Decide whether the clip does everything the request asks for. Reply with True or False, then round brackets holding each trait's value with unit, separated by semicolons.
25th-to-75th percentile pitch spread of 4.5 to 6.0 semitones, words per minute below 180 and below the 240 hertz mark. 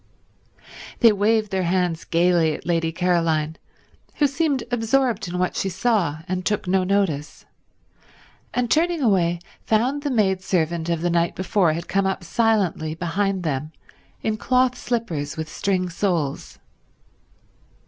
True (4.8 semitones; 140 wpm; 185 Hz)